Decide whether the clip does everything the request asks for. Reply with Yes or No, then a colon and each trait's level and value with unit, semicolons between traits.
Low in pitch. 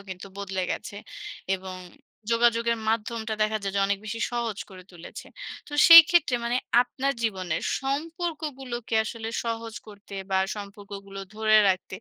No: high, 220 Hz